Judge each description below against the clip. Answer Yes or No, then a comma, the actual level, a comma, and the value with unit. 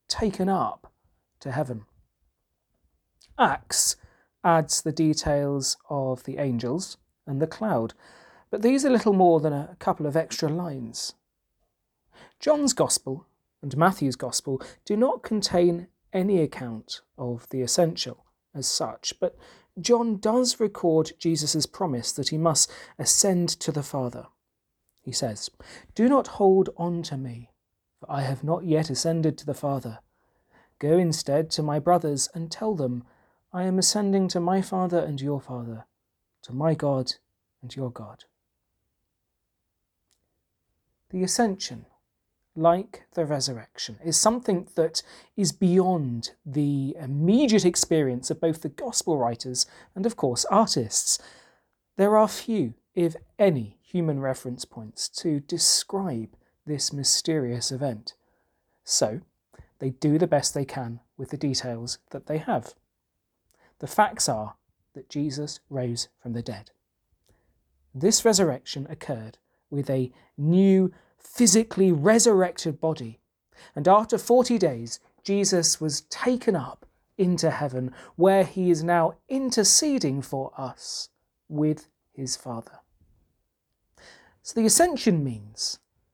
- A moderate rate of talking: No, slow, 125 wpm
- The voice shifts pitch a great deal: Yes, wide, 6.5 semitones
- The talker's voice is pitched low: No, medium, 155 Hz